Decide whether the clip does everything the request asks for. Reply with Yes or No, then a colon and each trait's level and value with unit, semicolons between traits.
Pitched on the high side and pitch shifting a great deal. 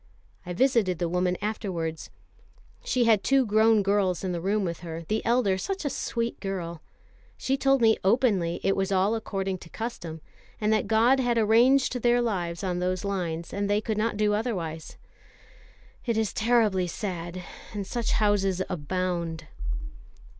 No: high, 200 Hz; average, 4.0 semitones